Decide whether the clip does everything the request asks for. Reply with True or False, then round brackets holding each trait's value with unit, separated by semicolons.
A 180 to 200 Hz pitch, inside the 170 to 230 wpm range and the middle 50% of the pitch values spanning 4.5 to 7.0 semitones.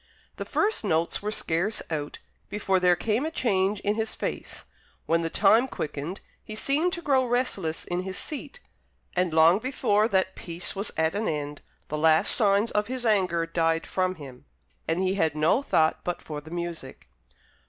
True (185 Hz; 180 wpm; 4.9 semitones)